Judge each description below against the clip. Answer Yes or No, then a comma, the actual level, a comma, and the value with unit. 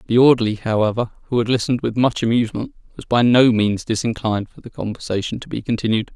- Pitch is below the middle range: Yes, low, 115 Hz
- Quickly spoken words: No, average, 195 wpm